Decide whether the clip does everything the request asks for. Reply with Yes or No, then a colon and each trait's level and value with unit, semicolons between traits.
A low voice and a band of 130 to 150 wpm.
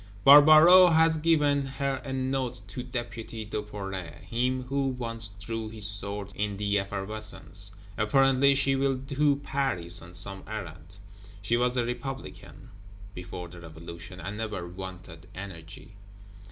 Yes: low, 110 Hz; slow, 135 wpm